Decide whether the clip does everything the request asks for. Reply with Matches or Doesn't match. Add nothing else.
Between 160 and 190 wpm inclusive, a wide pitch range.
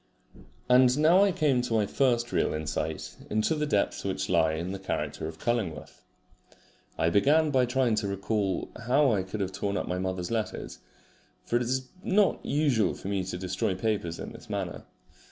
Matches